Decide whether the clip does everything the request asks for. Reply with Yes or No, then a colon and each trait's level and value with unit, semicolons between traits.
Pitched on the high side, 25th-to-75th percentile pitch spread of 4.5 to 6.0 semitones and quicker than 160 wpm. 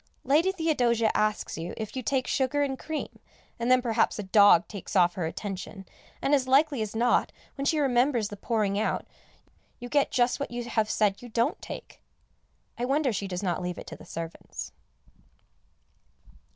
Yes: high, 235 Hz; average, 4.8 semitones; average, 180 wpm